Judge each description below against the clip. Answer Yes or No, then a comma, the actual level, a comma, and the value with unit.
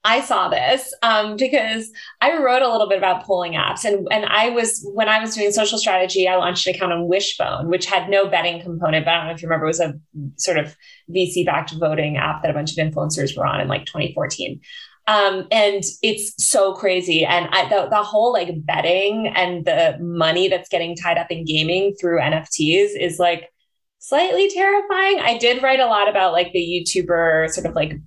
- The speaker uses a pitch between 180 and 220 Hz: Yes, medium, 185 Hz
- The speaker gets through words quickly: Yes, fast, 210 wpm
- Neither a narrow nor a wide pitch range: Yes, average, 4.2 semitones